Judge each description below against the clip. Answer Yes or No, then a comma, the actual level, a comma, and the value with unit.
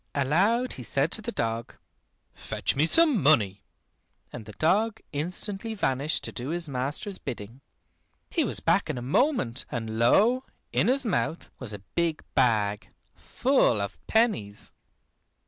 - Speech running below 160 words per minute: Yes, average, 145 wpm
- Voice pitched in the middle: Yes, medium, 145 Hz